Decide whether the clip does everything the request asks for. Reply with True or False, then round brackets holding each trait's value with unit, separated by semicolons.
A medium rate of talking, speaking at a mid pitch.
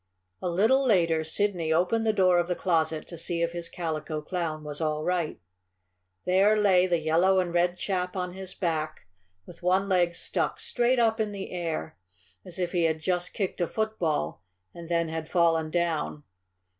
True (180 wpm; 175 Hz)